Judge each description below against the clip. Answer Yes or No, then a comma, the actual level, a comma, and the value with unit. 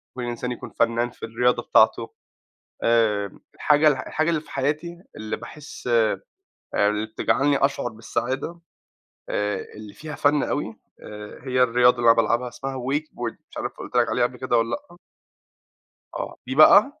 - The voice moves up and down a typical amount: Yes, average, 3.9 semitones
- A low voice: Yes, low, 125 Hz